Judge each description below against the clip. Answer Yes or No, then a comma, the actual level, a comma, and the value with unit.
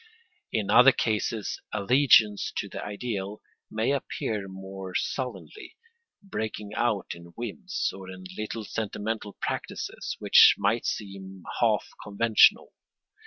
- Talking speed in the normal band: No, slow, 115 wpm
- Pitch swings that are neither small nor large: Yes, average, 3.1 semitones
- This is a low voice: Yes, low, 105 Hz